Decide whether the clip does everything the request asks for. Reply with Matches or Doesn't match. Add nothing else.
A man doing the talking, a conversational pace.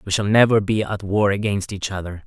Doesn't match